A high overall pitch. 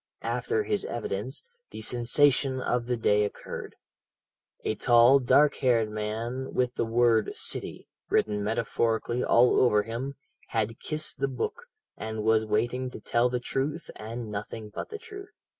No: low, 120 Hz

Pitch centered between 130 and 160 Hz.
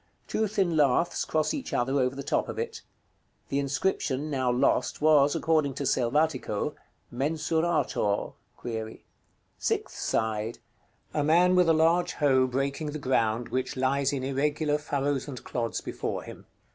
Yes: medium, 140 Hz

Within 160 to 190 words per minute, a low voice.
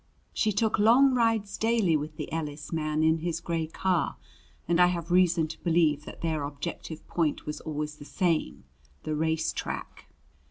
No: average, 170 wpm; medium, 165 Hz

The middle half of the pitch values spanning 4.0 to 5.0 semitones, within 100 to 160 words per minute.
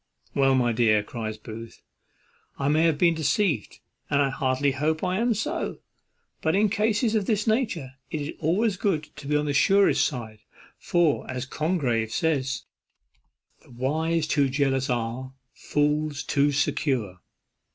Yes: average, 4.3 semitones; average, 150 wpm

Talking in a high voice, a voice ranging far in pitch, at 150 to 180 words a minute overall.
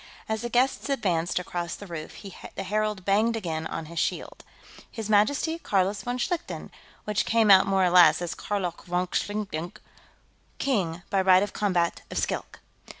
No: high, 195 Hz; average, 3.4 semitones; average, 165 wpm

